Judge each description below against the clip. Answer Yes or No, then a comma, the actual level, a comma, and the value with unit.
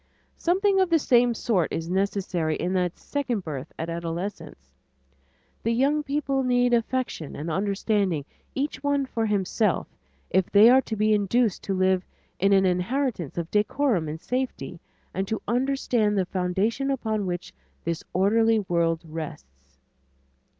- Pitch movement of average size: No, wide, 5.9 semitones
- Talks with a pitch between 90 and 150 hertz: No, high, 205 Hz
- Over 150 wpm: No, average, 145 wpm